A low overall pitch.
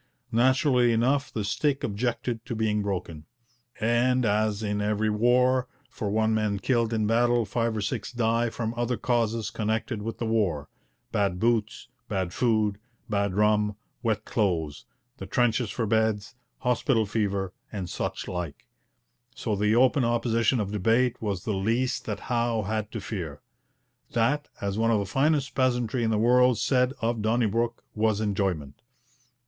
Yes: low, 110 Hz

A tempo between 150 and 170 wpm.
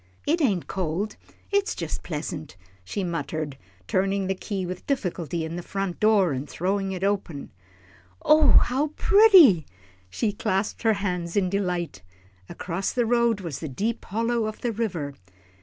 Yes: average, 160 wpm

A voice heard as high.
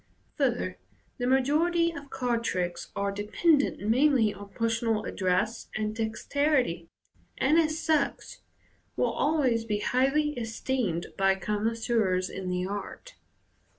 Yes: high, 230 Hz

